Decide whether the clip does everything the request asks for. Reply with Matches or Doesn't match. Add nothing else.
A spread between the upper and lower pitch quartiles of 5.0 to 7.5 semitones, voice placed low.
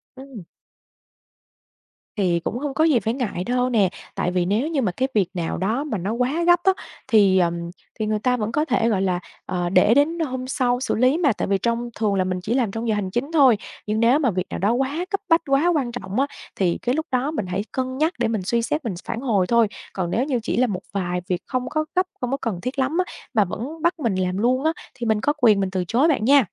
Doesn't match